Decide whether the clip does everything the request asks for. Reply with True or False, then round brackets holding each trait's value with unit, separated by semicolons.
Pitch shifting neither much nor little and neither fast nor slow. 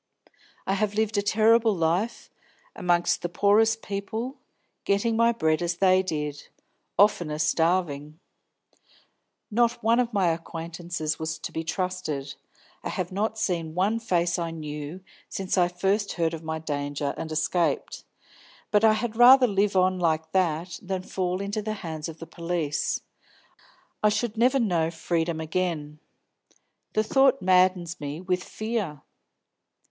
True (4.4 semitones; 145 wpm)